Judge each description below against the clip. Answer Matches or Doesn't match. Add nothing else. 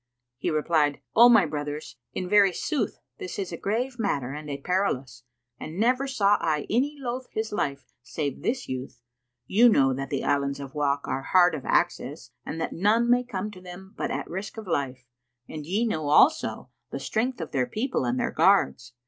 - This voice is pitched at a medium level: Matches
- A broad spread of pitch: Matches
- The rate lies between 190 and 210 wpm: Matches